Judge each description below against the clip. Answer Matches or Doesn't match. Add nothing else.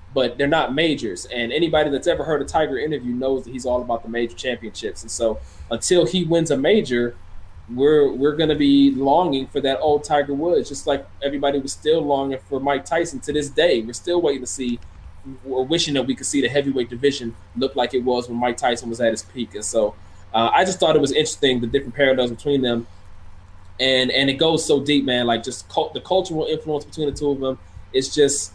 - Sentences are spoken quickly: Matches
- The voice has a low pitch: Matches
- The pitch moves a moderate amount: Matches